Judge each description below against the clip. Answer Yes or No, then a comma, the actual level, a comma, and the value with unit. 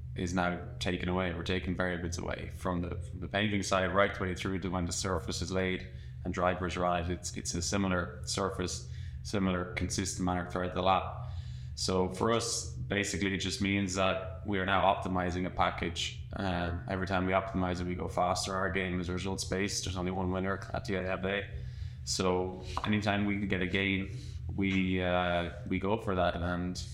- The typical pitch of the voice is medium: No, very low, 95 Hz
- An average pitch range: No, narrow, 1.5 semitones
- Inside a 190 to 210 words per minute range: Yes, average, 200 wpm